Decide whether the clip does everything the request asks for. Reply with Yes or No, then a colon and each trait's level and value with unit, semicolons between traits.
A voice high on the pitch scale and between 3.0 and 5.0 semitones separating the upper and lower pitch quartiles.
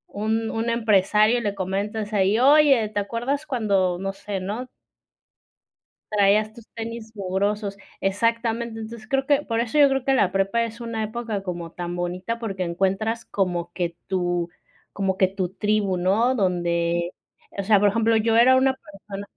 Yes: high, 210 Hz; average, 3.3 semitones